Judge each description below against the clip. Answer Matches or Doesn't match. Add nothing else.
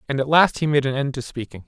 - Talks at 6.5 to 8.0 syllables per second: Matches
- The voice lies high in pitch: Doesn't match